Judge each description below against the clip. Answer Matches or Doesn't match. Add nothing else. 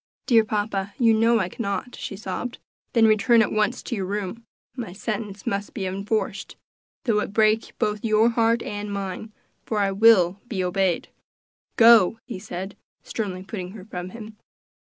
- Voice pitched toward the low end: Doesn't match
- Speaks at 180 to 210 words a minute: Doesn't match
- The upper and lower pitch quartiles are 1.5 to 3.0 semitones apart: Matches